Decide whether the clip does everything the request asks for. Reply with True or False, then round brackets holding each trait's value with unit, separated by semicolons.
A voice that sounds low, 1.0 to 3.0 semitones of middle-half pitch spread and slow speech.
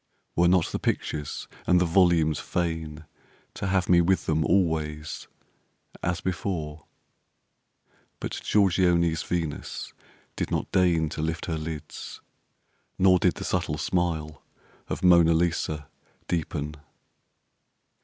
True (85 Hz; 2.4 semitones; 115 wpm)